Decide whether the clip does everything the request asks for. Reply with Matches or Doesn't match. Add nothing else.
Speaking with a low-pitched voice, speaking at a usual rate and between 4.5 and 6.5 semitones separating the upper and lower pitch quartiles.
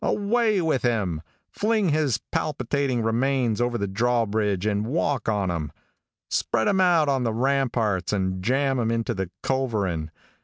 Matches